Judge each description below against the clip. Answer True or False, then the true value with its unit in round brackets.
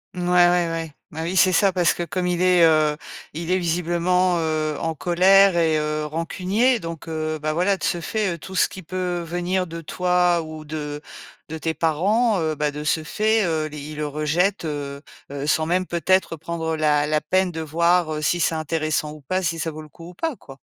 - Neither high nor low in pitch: True (165 Hz)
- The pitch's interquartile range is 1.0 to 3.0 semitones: True (2.6 semitones)